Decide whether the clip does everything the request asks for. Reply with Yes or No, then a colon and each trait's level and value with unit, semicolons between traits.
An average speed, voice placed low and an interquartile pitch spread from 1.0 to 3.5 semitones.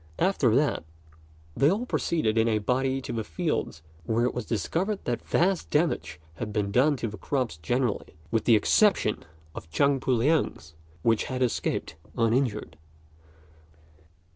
No: average, 150 wpm; low, 125 Hz; average, 4.8 semitones